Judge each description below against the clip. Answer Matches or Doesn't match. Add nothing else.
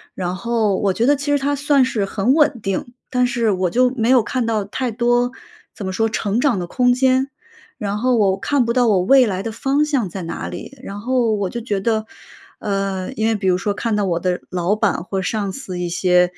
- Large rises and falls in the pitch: Doesn't match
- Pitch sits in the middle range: Doesn't match